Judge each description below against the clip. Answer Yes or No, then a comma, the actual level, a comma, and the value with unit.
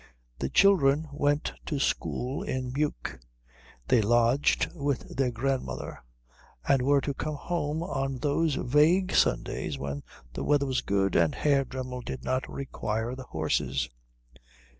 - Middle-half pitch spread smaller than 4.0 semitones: Yes, average, 3.5 semitones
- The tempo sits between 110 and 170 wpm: Yes, average, 140 wpm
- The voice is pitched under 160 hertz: Yes, low, 135 Hz